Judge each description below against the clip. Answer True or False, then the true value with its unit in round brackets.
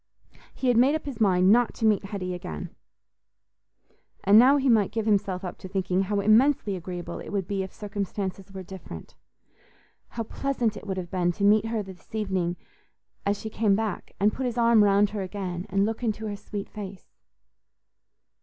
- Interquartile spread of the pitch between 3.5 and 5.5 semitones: False (2.7 semitones)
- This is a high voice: True (205 Hz)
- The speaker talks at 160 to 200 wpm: True (185 wpm)